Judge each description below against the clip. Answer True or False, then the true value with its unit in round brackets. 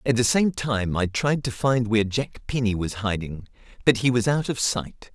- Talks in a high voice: False (115 Hz)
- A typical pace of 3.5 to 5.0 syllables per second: True (4.7 syllables/s)